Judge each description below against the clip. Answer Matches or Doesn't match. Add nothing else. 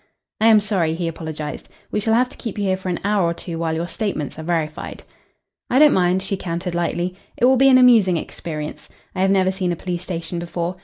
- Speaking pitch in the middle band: Matches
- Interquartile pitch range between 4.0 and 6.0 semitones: Doesn't match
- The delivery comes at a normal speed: Doesn't match